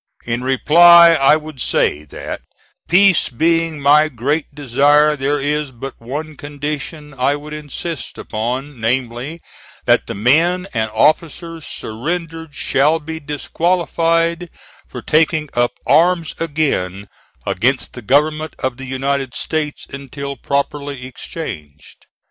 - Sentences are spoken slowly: Yes, slow, 120 wpm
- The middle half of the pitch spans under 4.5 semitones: Yes, average, 3.4 semitones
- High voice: No, medium, 145 Hz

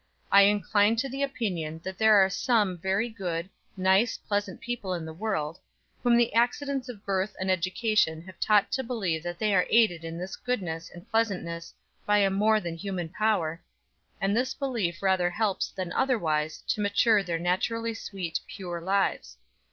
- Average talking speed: Yes, average, 175 wpm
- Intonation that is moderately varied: Yes, average, 4.1 semitones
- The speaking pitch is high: Yes, high, 195 Hz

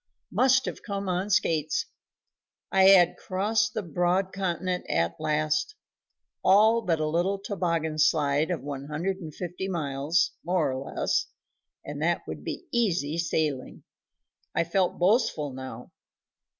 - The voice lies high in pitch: No, medium, 175 Hz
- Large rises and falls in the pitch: No, average, 4.0 semitones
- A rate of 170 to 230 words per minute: No, slow, 135 wpm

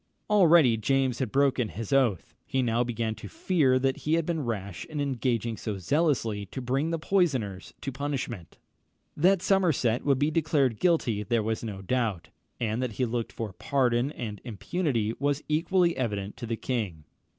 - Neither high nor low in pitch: No, low, 125 Hz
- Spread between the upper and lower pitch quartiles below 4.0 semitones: No, average, 4.8 semitones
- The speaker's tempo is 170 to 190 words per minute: Yes, average, 175 wpm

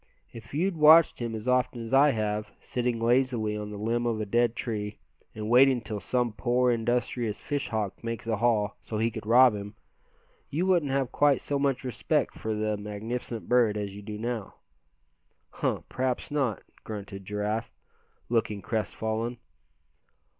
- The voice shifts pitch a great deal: No, average, 2.9 semitones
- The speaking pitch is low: Yes, low, 115 Hz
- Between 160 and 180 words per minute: Yes, average, 165 wpm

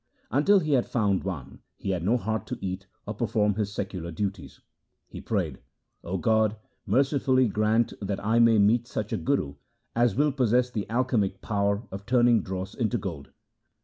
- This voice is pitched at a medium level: No, low, 110 Hz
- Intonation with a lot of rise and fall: No, average, 3.8 semitones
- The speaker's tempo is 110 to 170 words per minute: No, average, 180 wpm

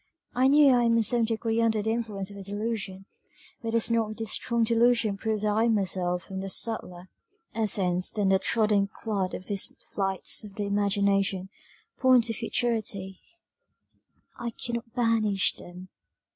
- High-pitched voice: Yes, high, 215 Hz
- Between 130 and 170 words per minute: Yes, average, 160 wpm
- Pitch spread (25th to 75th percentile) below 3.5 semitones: Yes, average, 2.9 semitones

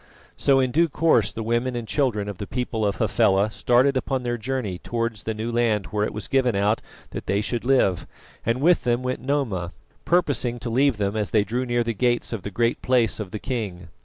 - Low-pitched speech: Yes, low, 115 Hz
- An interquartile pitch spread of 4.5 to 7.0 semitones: No, average, 3.4 semitones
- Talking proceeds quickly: Yes, fast, 220 wpm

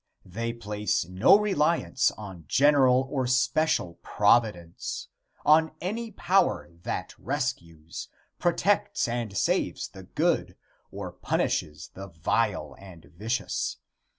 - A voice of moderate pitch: No, low, 115 Hz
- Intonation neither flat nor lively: No, wide, 9.0 semitones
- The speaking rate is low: Yes, slow, 105 wpm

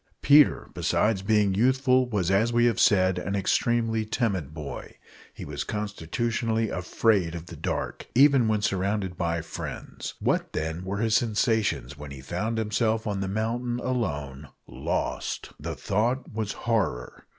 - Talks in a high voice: No, low, 105 Hz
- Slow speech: No, average, 150 wpm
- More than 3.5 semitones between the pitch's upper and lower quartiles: Yes, average, 4.1 semitones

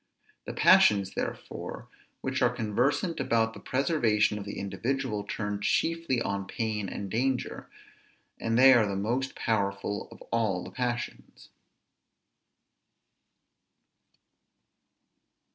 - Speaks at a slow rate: Yes, slow, 110 wpm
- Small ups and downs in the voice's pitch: No, average, 4.1 semitones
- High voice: No, low, 115 Hz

